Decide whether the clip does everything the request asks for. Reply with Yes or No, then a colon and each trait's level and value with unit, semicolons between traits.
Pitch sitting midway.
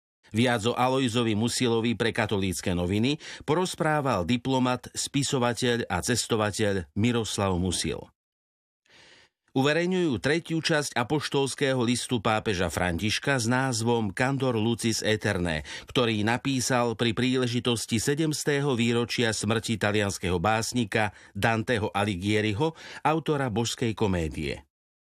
No: low, 120 Hz